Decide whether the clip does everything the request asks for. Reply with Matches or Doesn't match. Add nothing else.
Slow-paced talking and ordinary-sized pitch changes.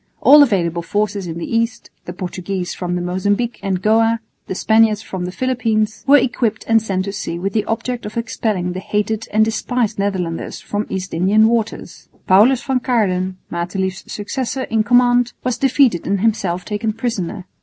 Doesn't match